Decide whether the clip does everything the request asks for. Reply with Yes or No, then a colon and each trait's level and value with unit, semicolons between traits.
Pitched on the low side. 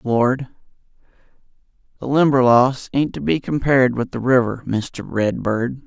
Yes: low, 125 Hz